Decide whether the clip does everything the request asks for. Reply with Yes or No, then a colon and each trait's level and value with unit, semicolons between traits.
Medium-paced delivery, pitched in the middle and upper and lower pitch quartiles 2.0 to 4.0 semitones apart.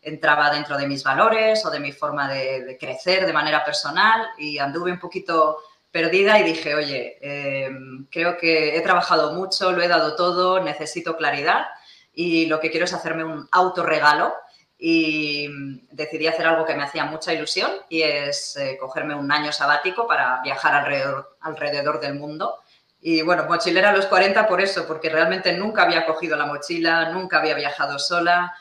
Yes: average, 175 wpm; medium, 160 Hz; average, 2.9 semitones